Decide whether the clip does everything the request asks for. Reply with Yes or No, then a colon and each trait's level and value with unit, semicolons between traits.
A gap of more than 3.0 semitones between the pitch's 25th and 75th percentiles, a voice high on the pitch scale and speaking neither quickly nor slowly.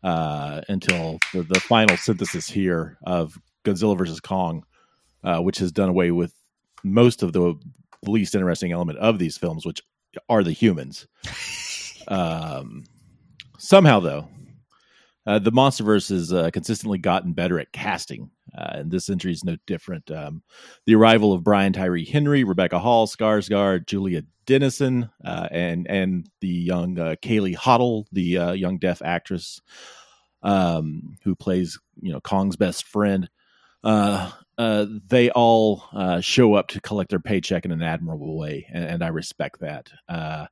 No: average, 3.7 semitones; very low, 95 Hz; average, 155 wpm